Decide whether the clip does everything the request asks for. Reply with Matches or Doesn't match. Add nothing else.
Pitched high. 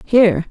Matches